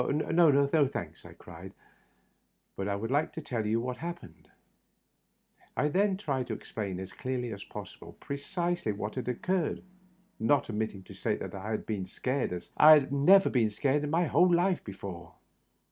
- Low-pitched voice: Yes, low, 130 Hz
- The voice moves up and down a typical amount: No, wide, 7.4 semitones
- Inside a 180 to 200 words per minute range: Yes, average, 185 wpm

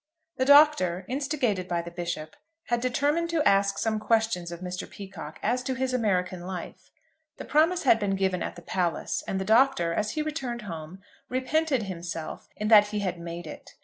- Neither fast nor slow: Yes, average, 185 wpm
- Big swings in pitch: Yes, wide, 6.4 semitones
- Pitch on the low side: No, high, 205 Hz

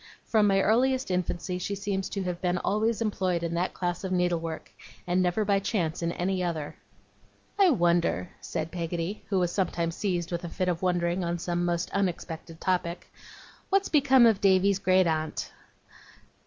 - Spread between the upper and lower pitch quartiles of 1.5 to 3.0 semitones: Yes, narrow, 2.5 semitones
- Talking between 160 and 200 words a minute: Yes, average, 175 wpm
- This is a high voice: No, medium, 180 Hz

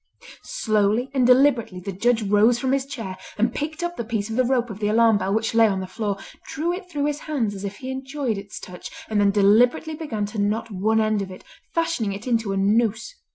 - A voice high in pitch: Yes, high, 225 Hz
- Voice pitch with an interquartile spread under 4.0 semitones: No, average, 4.3 semitones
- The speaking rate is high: Yes, fast, 235 wpm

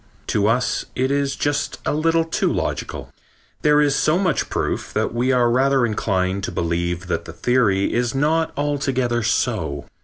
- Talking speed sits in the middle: Yes, average, 165 wpm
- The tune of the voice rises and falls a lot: Yes, wide, 5.9 semitones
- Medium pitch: No, low, 130 Hz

